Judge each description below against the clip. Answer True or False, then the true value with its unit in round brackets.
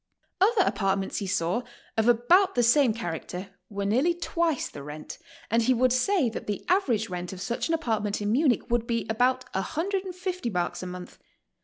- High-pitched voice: True (235 Hz)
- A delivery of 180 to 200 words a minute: True (185 wpm)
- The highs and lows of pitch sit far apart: True (8.2 semitones)